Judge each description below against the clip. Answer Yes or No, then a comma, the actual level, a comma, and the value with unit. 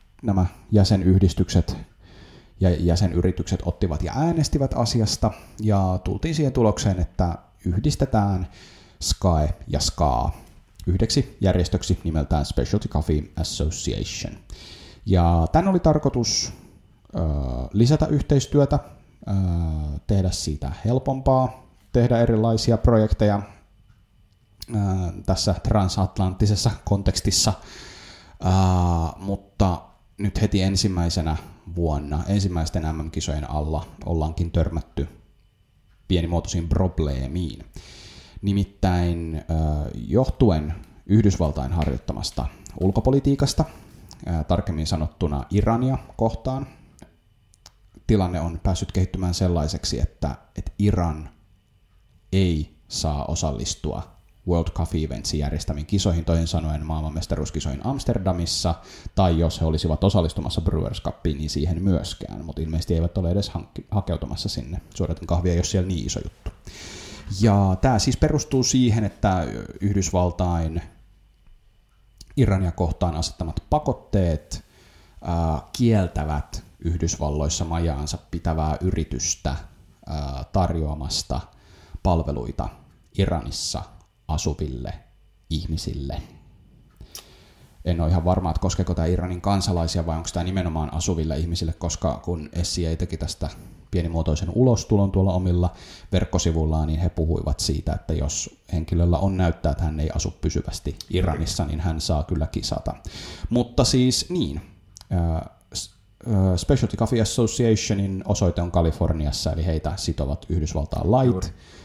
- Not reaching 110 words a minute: Yes, average, 100 wpm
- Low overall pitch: Yes, very low, 90 Hz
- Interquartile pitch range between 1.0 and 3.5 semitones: No, average, 3.9 semitones